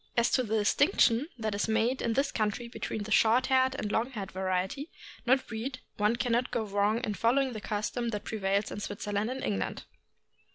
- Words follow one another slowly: No, average, 200 wpm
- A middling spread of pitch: Yes, average, 3.4 semitones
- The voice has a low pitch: No, high, 225 Hz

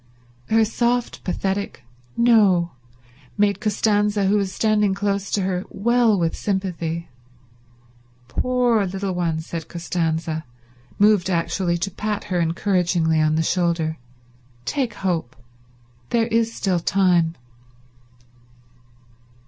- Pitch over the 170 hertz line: Yes, high, 190 Hz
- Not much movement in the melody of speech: No, average, 3.7 semitones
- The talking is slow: Yes, slow, 110 wpm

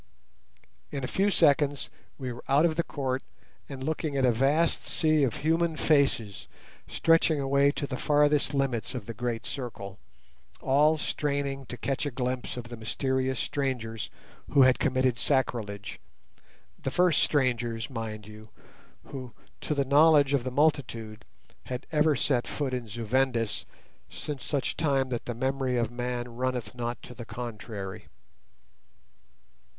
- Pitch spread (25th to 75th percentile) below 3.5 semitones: Yes, average, 3.1 semitones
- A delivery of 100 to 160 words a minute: Yes, average, 150 wpm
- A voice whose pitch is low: Yes, low, 130 Hz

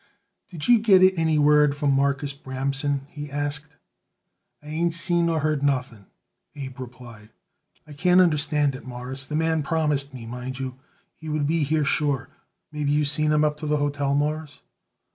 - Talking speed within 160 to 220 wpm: Yes, average, 175 wpm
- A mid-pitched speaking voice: Yes, medium, 145 Hz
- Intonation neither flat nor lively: No, narrow, 2.1 semitones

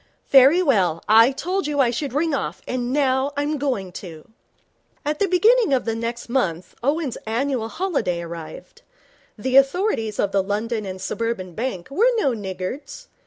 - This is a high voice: Yes, very high, 250 Hz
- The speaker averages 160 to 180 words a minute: Yes, average, 165 wpm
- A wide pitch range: Yes, wide, 5.9 semitones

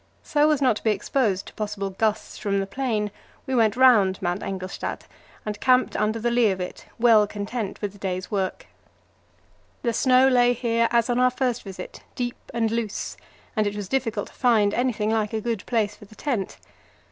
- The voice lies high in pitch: Yes, high, 220 Hz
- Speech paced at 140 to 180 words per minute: No, average, 195 wpm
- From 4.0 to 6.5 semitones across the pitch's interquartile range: No, average, 3.2 semitones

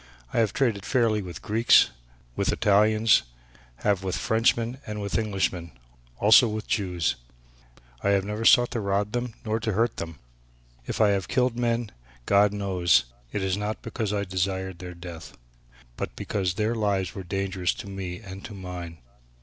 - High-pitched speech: No, low, 100 Hz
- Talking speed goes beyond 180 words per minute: No, average, 165 wpm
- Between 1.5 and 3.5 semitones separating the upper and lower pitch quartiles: Yes, average, 2.8 semitones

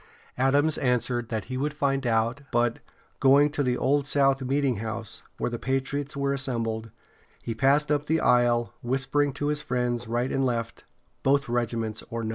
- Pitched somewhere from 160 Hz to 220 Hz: No, low, 130 Hz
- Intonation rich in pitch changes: No, average, 2.9 semitones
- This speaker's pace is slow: No, average, 170 wpm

